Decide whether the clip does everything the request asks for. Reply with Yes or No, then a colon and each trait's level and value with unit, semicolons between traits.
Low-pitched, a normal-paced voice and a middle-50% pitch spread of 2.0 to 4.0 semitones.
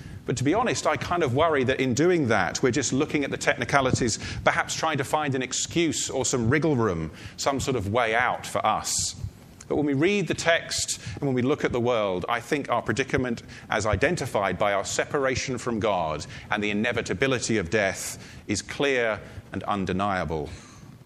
No: low, 130 Hz; average, 195 wpm; average, 4.5 semitones